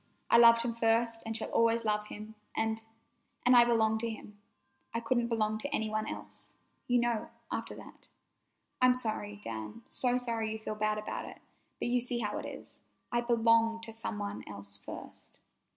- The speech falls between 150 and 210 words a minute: Yes, average, 180 wpm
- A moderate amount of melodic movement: No, narrow, 1.6 semitones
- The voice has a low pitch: No, high, 225 Hz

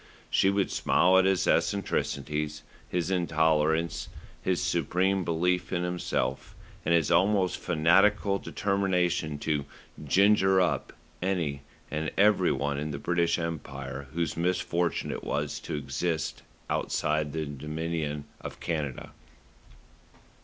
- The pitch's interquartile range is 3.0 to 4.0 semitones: Yes, average, 3.5 semitones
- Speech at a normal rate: No, slow, 115 wpm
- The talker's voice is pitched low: Yes, very low, 85 Hz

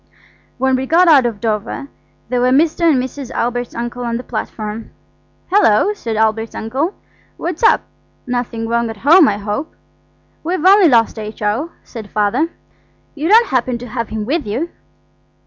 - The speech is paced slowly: No, average, 165 wpm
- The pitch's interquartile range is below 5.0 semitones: No, wide, 5.6 semitones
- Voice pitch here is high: Yes, high, 245 Hz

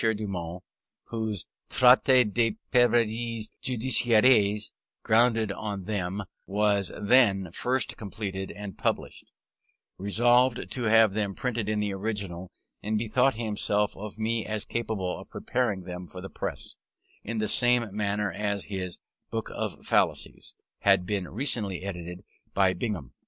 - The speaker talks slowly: Yes, slow, 130 wpm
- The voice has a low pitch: Yes, low, 105 Hz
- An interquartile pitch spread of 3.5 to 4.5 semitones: No, average, 2.9 semitones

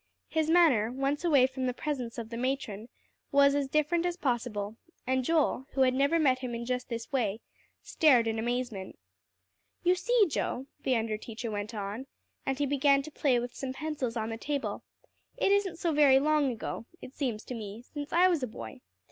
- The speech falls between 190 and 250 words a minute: Yes, average, 200 wpm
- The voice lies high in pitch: Yes, very high, 260 Hz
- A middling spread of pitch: Yes, average, 4.1 semitones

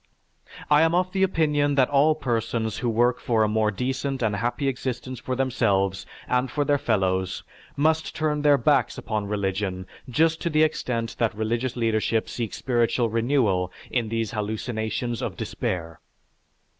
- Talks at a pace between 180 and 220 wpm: No, average, 160 wpm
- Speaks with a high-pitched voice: No, low, 120 Hz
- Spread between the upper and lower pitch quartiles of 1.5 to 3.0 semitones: No, average, 4.5 semitones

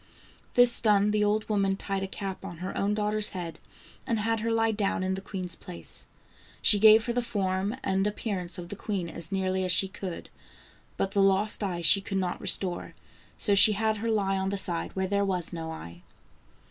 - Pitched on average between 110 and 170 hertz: No, high, 195 Hz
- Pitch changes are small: Yes, narrow, 2.2 semitones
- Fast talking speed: Yes, fast, 210 wpm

